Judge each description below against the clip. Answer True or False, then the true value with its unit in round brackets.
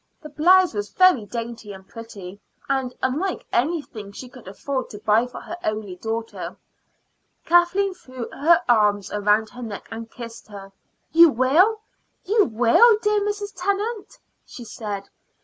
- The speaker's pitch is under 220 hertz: False (245 Hz)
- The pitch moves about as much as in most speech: False (8.6 semitones)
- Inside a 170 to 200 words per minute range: False (150 wpm)